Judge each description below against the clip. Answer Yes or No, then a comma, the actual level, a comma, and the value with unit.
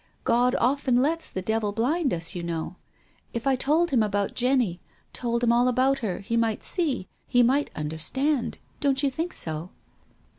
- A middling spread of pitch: Yes, average, 5.0 semitones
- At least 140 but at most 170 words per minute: No, average, 180 wpm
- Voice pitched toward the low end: No, high, 245 Hz